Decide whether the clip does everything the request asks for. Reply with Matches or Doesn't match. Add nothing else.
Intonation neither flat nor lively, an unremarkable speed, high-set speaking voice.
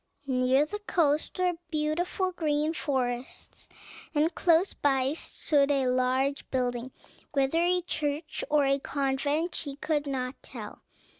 Doesn't match